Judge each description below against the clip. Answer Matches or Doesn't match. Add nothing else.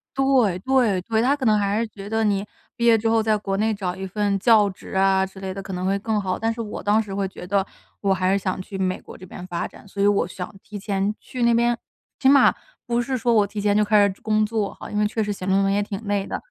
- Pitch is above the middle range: Matches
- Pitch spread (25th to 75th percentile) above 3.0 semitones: Doesn't match